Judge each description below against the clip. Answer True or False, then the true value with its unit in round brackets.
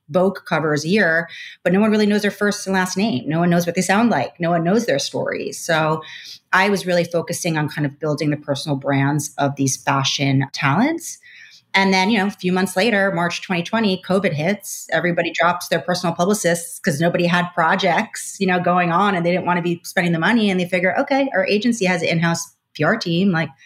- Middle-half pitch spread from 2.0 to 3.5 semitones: True (2.9 semitones)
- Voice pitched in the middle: True (175 Hz)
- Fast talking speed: True (225 wpm)